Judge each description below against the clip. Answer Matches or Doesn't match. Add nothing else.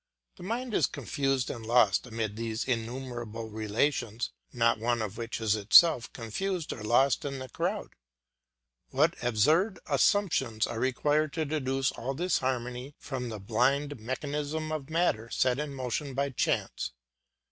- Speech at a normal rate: Matches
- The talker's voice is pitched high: Doesn't match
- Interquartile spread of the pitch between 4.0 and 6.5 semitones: Matches